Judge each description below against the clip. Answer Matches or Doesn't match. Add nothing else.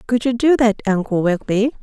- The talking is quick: Doesn't match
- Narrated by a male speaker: Doesn't match